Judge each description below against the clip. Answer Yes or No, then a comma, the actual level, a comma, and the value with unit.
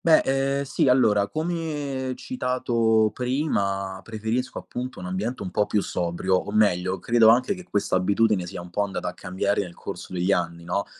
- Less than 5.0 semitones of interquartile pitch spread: No, average, 5.3 semitones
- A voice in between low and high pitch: No, low, 110 Hz